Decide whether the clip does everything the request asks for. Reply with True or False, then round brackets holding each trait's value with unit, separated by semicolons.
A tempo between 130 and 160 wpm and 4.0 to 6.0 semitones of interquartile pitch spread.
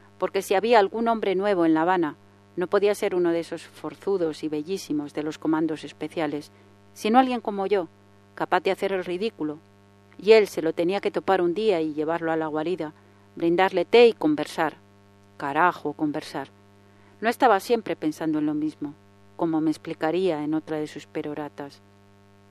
False (175 wpm; 4.3 semitones)